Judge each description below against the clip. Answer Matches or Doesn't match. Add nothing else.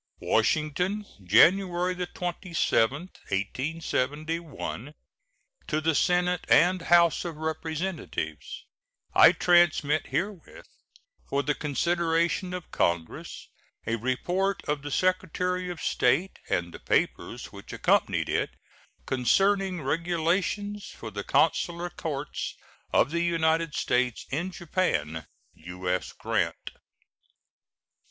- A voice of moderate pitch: Matches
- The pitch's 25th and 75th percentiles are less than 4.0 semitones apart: Doesn't match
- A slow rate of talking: Matches